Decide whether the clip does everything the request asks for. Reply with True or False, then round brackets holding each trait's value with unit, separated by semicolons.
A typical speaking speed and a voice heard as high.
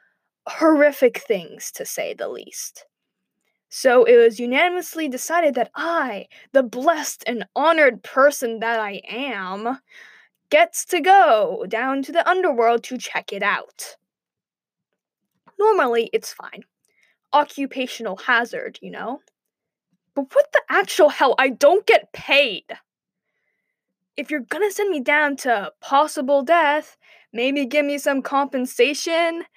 False (125 wpm; 290 Hz)